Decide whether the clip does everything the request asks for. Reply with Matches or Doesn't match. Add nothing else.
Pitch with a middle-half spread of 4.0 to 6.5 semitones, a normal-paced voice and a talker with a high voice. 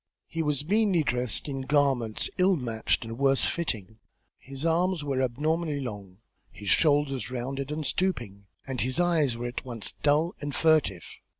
Doesn't match